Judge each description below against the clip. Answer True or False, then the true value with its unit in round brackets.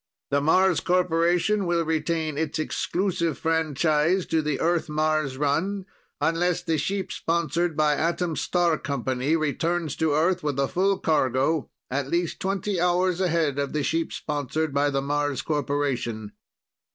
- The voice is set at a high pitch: False (160 Hz)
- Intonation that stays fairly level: False (3.1 semitones)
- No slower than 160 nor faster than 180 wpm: False (145 wpm)